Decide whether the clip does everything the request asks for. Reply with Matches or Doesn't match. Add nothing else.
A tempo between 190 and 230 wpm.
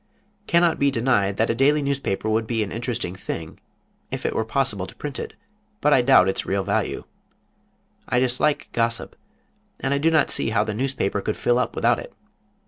Matches